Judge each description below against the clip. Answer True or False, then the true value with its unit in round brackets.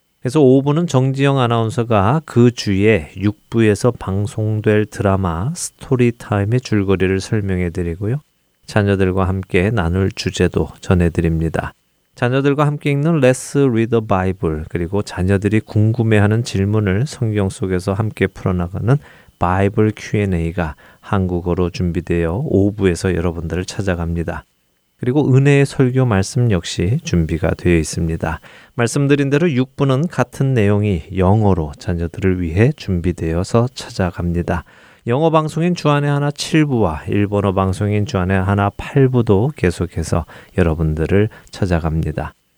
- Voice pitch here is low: True (100 Hz)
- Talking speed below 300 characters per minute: False (325 characters per minute)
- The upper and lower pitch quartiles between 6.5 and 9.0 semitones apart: False (5.6 semitones)